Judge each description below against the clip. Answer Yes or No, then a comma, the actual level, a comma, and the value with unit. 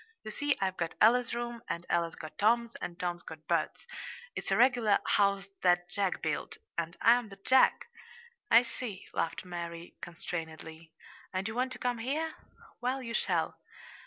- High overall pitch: Yes, high, 200 Hz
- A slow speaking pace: No, average, 165 wpm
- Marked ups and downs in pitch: Yes, wide, 5.9 semitones